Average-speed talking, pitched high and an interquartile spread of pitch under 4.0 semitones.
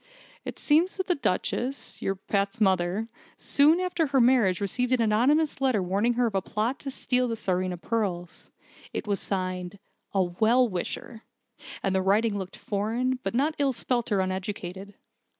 No: average, 170 wpm; high, 220 Hz; average, 5.0 semitones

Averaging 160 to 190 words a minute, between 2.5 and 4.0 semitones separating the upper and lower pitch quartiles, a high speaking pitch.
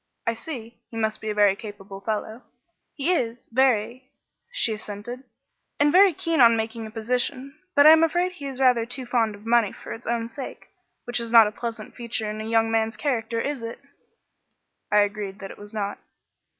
No: average, 200 wpm; average, 2.9 semitones; high, 230 Hz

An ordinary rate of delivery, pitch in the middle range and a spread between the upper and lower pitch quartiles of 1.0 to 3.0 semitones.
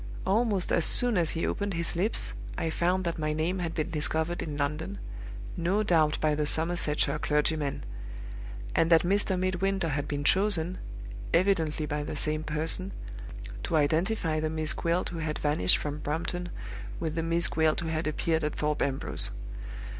Yes: average, 170 wpm; medium, 160 Hz; narrow, 2.6 semitones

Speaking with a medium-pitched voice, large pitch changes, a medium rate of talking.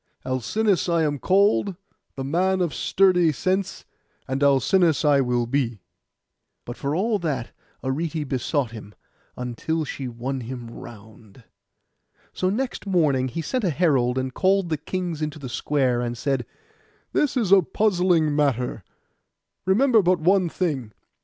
Yes: medium, 150 Hz; wide, 6.2 semitones; average, 145 wpm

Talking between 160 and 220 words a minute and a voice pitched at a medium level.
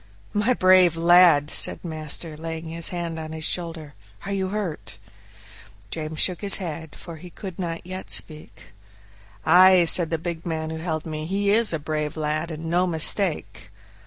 Yes: average, 170 wpm; medium, 165 Hz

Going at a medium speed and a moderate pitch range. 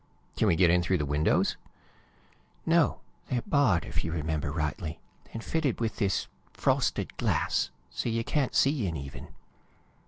No: average, 155 wpm; wide, 7.6 semitones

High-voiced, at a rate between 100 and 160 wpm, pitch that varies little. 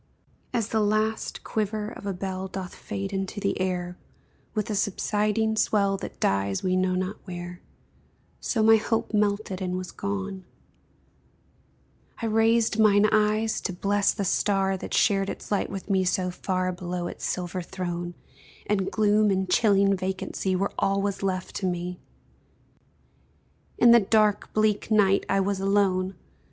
Yes: high, 195 Hz; average, 155 wpm; narrow, 2.3 semitones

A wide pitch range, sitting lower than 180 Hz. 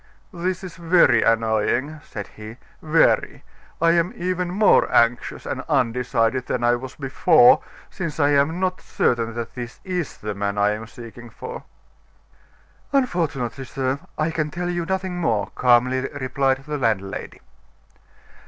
Yes: wide, 6.5 semitones; low, 135 Hz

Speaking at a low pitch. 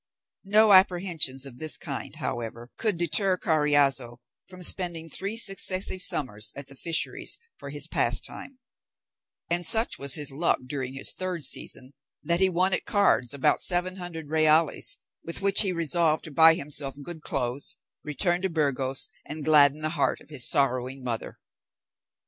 No: medium, 155 Hz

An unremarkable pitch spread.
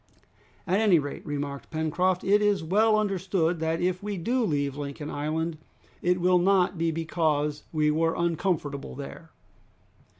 Yes: average, 3.6 semitones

